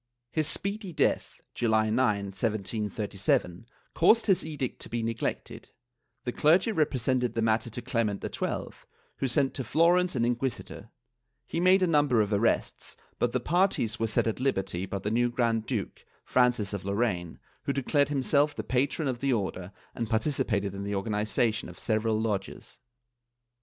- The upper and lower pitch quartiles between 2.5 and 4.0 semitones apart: No, average, 4.6 semitones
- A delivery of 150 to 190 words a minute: Yes, average, 170 wpm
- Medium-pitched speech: No, low, 120 Hz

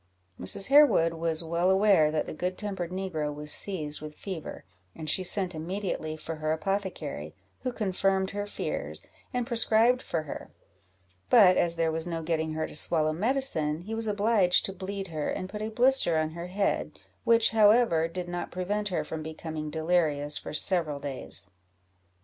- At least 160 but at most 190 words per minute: Yes, average, 175 wpm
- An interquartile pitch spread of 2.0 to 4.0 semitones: No, average, 4.4 semitones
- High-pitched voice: No, medium, 175 Hz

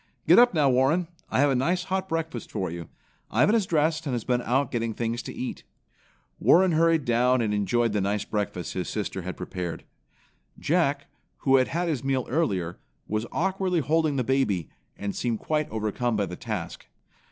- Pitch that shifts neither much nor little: No, wide, 7.0 semitones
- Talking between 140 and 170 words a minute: No, average, 185 wpm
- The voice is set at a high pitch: No, low, 130 Hz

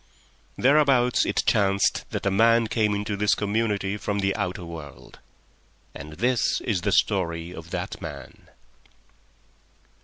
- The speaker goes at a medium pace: No, slow, 130 wpm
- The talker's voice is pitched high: No, low, 100 Hz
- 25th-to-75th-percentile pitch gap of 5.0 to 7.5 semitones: No, average, 3.6 semitones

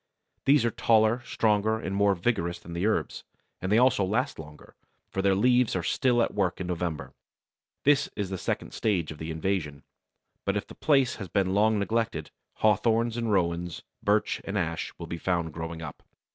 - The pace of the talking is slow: No, average, 185 wpm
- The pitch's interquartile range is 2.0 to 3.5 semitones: No, average, 4.5 semitones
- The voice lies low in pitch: Yes, low, 100 Hz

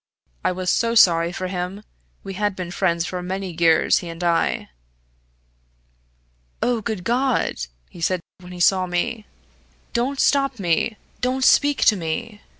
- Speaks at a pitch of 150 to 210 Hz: Yes, medium, 185 Hz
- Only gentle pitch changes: No, average, 4.7 semitones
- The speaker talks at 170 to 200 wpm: No, average, 150 wpm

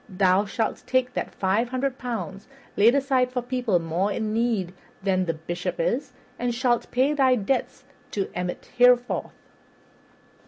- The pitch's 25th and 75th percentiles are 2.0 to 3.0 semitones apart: No, average, 4.7 semitones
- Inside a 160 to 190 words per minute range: No, average, 150 wpm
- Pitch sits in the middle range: No, high, 235 Hz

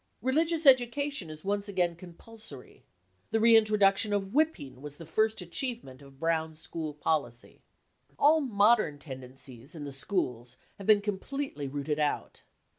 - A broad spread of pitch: Yes, wide, 7.4 semitones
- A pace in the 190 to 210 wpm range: No, average, 140 wpm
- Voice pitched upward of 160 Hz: Yes, medium, 185 Hz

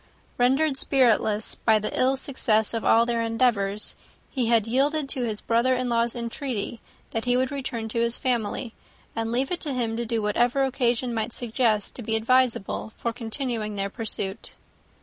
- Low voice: No, high, 235 Hz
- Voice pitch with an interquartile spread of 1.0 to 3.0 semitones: Yes, narrow, 2.4 semitones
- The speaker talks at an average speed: Yes, average, 175 wpm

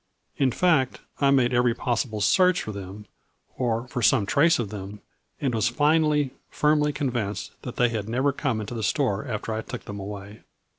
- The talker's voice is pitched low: Yes, low, 120 Hz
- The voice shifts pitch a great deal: No, average, 4.8 semitones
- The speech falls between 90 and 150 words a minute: No, average, 185 wpm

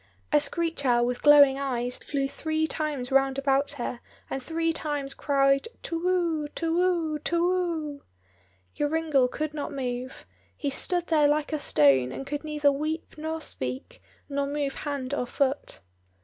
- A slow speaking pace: No, average, 160 wpm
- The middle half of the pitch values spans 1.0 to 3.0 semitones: Yes, average, 2.7 semitones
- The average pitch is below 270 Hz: No, very high, 290 Hz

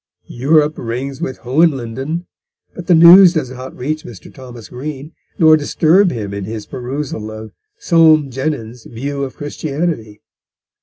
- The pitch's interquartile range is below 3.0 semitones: No, average, 4.5 semitones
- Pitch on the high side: No, low, 135 Hz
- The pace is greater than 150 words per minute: No, average, 140 wpm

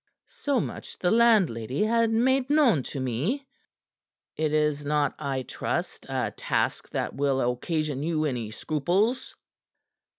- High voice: No, medium, 155 Hz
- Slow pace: Yes, slow, 130 wpm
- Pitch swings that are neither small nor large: No, wide, 9.0 semitones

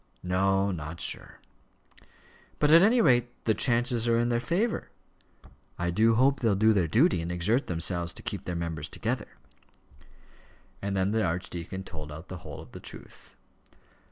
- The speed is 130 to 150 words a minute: No, average, 165 wpm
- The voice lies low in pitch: Yes, low, 100 Hz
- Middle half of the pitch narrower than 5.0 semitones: No, wide, 5.5 semitones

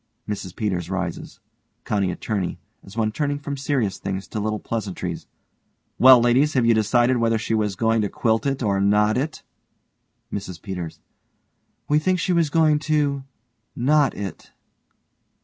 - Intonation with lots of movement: Yes, wide, 5.9 semitones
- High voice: No, low, 110 Hz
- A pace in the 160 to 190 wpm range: No, average, 150 wpm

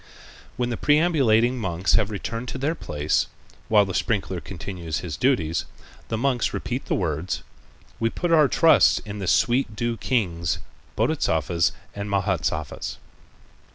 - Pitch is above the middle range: No, low, 105 Hz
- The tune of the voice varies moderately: No, wide, 5.9 semitones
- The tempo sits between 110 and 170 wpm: Yes, average, 140 wpm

